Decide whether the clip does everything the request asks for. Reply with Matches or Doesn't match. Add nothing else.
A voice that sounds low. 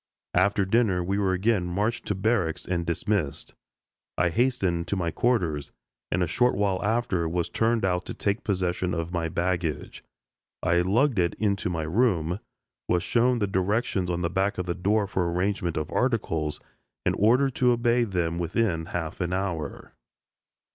Matches